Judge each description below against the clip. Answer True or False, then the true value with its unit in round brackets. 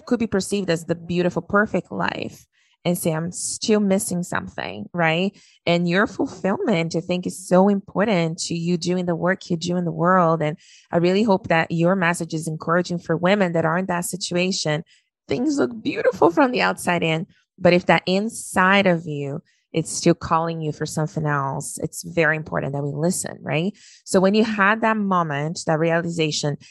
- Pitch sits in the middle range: True (175 Hz)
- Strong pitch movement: False (2.8 semitones)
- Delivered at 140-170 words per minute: False (190 wpm)